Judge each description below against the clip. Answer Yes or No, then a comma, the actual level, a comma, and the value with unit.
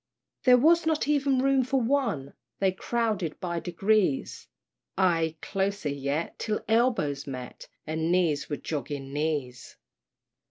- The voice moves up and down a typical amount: No, wide, 8.3 semitones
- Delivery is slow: Yes, slow, 125 wpm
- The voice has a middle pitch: Yes, medium, 180 Hz